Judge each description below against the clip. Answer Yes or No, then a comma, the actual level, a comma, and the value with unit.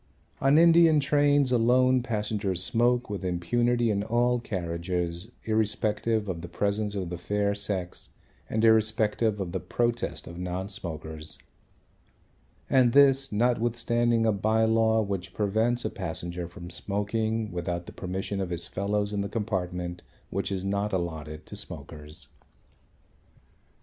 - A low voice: Yes, low, 105 Hz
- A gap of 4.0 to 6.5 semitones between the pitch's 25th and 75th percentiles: Yes, average, 4.5 semitones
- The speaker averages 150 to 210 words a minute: No, slow, 135 wpm